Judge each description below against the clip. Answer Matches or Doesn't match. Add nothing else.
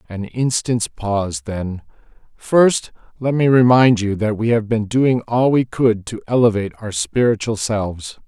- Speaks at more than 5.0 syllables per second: Doesn't match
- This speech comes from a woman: Doesn't match